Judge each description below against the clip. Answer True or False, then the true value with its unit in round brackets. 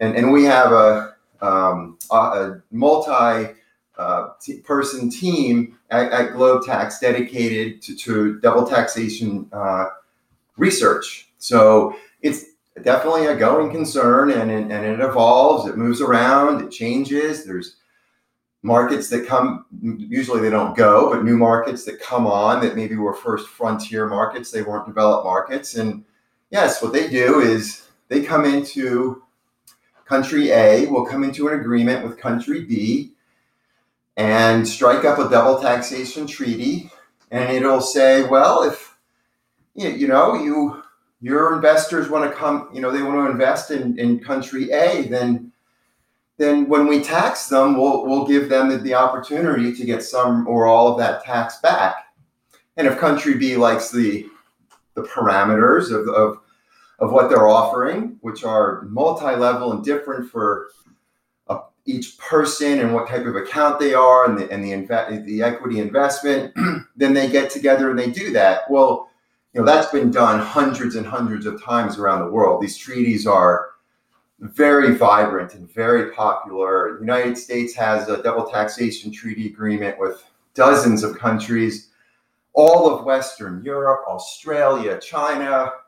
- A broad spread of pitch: False (3.9 semitones)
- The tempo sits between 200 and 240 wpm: False (150 wpm)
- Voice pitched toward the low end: True (125 Hz)